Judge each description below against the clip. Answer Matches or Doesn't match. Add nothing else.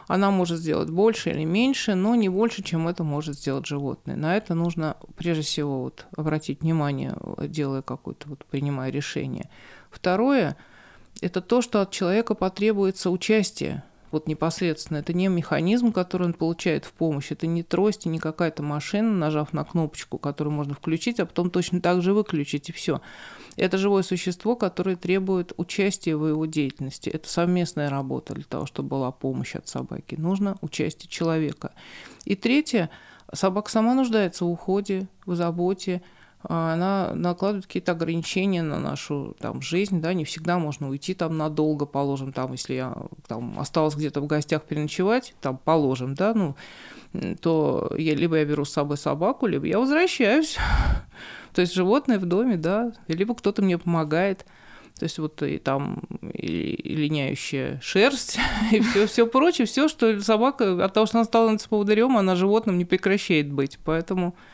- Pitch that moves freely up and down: Doesn't match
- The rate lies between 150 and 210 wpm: Matches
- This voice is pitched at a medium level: Matches